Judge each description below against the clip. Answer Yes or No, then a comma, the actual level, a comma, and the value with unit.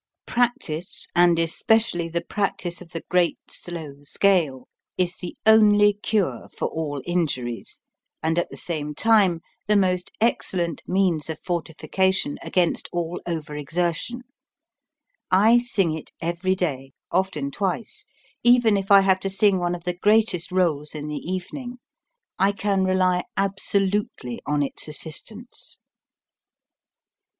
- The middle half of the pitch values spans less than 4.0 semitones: Yes, average, 3.5 semitones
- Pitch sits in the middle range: Yes, medium, 180 Hz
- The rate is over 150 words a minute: No, slow, 135 wpm